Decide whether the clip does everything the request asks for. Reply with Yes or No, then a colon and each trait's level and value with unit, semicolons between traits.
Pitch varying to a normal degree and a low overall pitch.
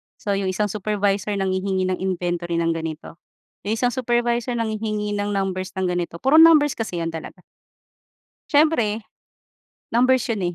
No: average, 4.1 semitones; high, 205 Hz